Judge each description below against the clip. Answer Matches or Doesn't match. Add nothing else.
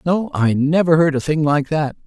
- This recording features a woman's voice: Doesn't match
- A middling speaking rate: Doesn't match